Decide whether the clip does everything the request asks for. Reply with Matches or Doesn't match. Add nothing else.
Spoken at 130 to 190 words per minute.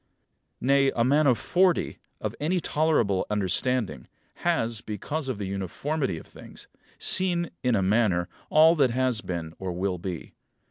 Matches